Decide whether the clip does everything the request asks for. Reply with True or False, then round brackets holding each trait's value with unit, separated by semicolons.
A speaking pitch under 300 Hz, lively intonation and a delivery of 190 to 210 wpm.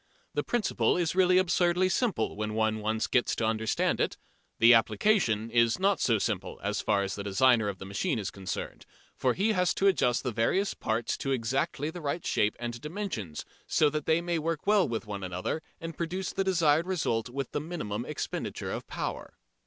True (135 Hz; 8.1 semitones; 195 wpm)